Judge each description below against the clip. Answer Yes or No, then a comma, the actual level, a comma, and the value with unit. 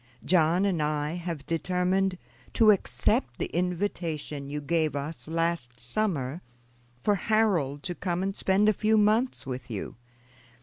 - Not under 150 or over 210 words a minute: No, average, 140 wpm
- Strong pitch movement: No, average, 4.7 semitones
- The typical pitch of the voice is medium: Yes, medium, 170 Hz